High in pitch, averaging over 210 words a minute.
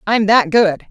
No: high, 205 Hz; average, 200 wpm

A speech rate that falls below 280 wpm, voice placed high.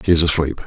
No: fast, 270 wpm; very low, 80 Hz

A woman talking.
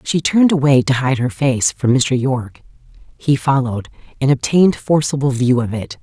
Yes: female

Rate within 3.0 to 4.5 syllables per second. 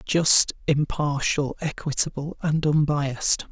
Yes: 3.8 syllables/s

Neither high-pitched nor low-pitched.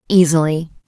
Yes: medium, 165 Hz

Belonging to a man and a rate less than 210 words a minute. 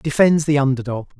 Yes: male; average, 200 wpm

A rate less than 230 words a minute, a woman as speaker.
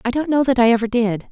No: fast, 320 wpm; female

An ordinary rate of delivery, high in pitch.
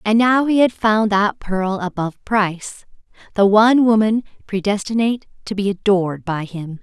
Yes: average, 160 wpm; high, 205 Hz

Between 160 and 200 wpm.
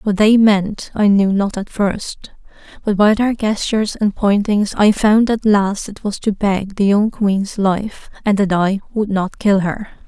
Yes: average, 195 wpm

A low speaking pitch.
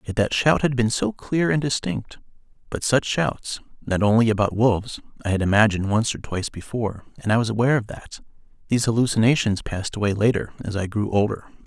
Yes: low, 115 Hz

